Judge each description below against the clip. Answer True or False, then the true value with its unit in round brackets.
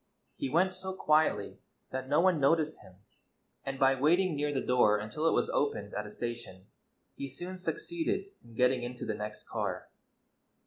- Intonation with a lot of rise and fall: True (6.2 semitones)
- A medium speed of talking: True (175 wpm)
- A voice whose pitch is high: False (135 Hz)